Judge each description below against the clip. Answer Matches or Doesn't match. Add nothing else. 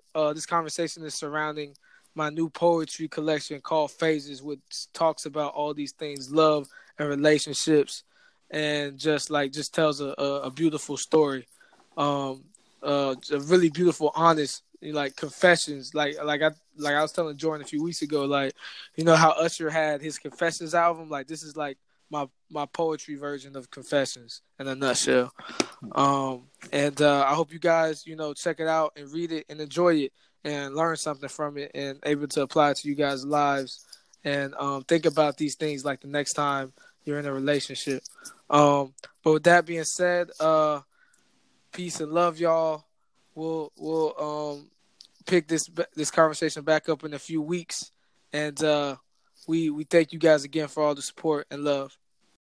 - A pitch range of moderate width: Doesn't match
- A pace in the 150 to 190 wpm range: Matches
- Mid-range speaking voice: Matches